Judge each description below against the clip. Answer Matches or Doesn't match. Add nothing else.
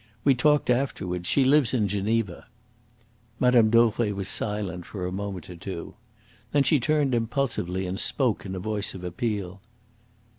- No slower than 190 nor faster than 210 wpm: Doesn't match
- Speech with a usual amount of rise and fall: Matches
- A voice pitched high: Doesn't match